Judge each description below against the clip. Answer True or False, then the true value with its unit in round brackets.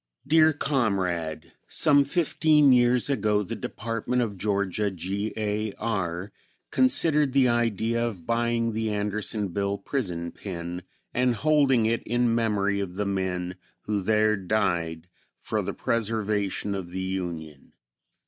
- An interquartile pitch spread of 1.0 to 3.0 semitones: False (3.9 semitones)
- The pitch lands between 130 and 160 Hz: False (105 Hz)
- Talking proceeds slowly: True (130 wpm)